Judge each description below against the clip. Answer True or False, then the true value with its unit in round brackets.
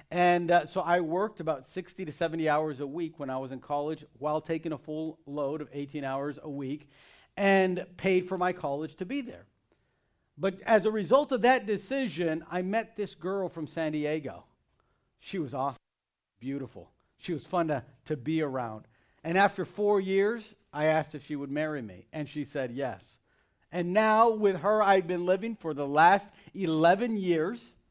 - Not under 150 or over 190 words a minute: True (185 wpm)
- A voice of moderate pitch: True (165 Hz)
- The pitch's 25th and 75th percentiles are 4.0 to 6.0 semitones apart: True (4.5 semitones)